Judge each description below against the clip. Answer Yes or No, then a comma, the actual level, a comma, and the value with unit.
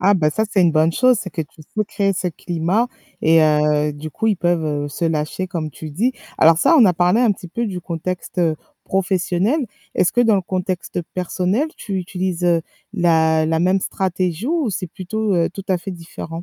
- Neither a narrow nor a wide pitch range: Yes, average, 3.2 semitones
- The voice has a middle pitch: Yes, medium, 180 Hz